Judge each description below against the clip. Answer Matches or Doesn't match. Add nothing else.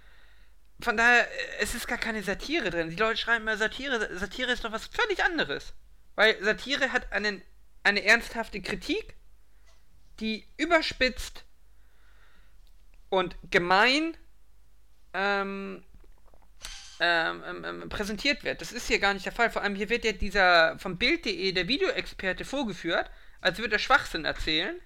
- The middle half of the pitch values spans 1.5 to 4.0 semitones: Doesn't match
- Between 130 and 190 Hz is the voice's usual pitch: Doesn't match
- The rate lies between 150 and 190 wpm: Doesn't match